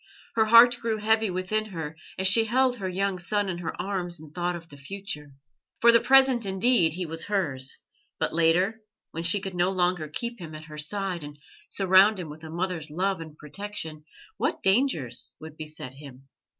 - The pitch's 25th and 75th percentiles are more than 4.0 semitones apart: Yes, average, 4.7 semitones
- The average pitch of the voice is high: No, medium, 180 Hz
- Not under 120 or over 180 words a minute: No, average, 190 wpm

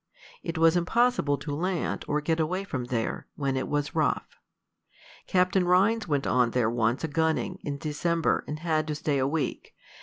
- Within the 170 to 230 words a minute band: Yes, average, 180 wpm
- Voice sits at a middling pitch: Yes, medium, 155 Hz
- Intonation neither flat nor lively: Yes, average, 3.8 semitones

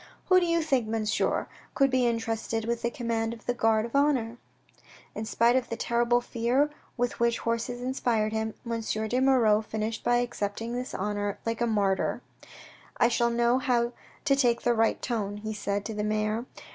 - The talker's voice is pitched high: Yes, high, 230 Hz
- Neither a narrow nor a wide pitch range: No, narrow, 1.9 semitones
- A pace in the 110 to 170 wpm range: No, average, 190 wpm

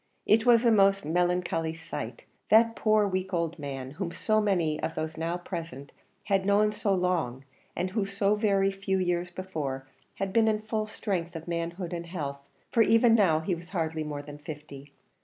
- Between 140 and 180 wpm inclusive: No, average, 190 wpm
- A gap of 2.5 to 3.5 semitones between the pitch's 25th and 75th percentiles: No, average, 4.0 semitones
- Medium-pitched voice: Yes, medium, 180 Hz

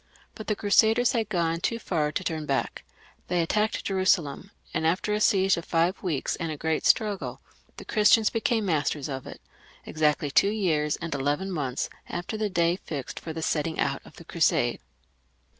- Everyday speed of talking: Yes, average, 180 wpm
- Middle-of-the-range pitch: Yes, medium, 170 Hz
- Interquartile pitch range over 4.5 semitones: Yes, average, 4.9 semitones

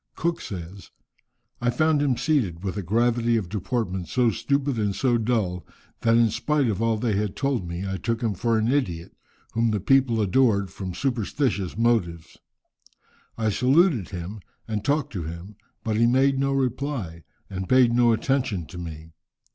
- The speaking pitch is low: Yes, low, 115 Hz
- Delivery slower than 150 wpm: No, average, 170 wpm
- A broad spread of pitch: No, average, 5.0 semitones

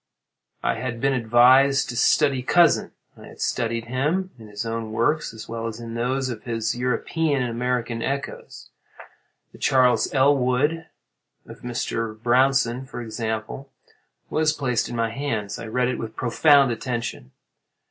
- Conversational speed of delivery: Yes, average, 145 wpm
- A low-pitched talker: Yes, low, 125 Hz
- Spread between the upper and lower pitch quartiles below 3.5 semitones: Yes, average, 2.9 semitones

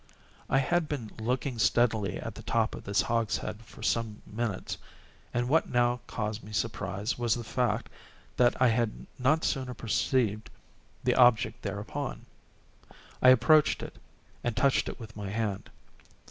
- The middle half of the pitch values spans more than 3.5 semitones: No, average, 2.8 semitones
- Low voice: Yes, low, 115 Hz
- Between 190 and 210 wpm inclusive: No, average, 150 wpm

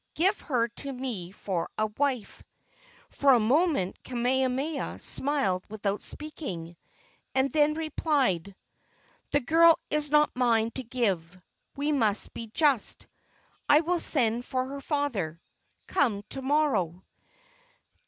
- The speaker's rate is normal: No, slow, 125 wpm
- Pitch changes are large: Yes, wide, 5.7 semitones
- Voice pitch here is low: No, very high, 255 Hz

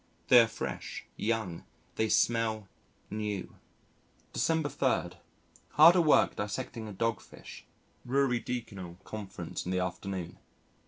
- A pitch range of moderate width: Yes, average, 4.5 semitones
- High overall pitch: No, low, 110 Hz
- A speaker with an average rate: No, slow, 110 wpm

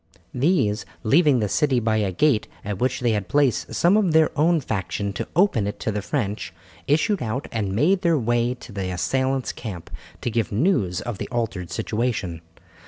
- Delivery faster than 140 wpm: Yes, average, 185 wpm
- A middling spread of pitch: No, wide, 6.0 semitones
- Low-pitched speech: Yes, low, 120 Hz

